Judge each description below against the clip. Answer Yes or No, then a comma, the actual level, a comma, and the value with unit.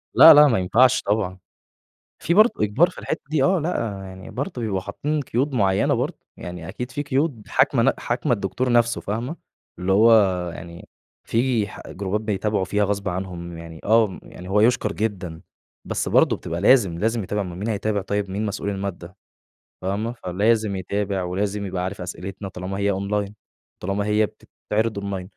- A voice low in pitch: Yes, low, 105 Hz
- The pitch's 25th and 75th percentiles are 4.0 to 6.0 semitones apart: No, average, 3.5 semitones